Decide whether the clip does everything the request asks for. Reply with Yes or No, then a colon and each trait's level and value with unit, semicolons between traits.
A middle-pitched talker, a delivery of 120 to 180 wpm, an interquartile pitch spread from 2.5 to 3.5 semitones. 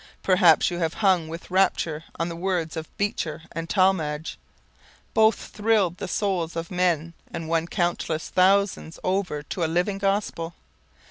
Yes: medium, 175 Hz; average, 150 wpm; average, 2.9 semitones